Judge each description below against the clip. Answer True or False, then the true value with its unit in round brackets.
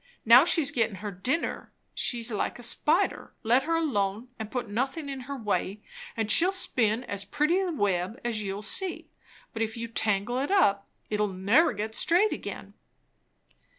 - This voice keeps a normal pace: True (170 wpm)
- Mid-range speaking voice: False (230 Hz)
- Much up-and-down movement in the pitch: True (5.7 semitones)